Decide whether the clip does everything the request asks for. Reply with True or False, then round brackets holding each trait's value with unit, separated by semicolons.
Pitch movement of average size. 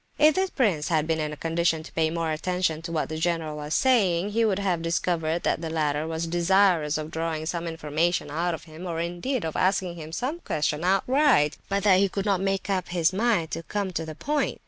True (3.4 semitones)